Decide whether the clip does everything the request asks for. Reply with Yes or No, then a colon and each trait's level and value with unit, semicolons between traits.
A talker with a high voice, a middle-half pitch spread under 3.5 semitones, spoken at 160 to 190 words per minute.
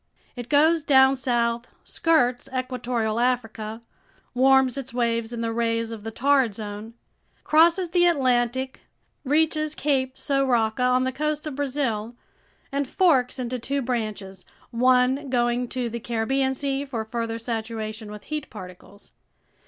No: very high, 250 Hz; average, 3.0 semitones; average, 140 wpm